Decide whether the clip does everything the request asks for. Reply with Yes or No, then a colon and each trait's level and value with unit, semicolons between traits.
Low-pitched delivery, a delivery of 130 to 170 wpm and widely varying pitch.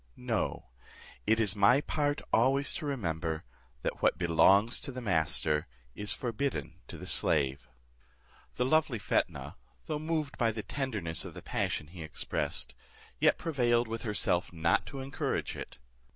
Yes: low, 115 Hz; average, 150 wpm; wide, 8.0 semitones